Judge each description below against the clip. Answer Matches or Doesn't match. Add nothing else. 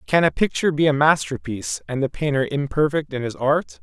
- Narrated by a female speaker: Doesn't match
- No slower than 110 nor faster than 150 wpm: Doesn't match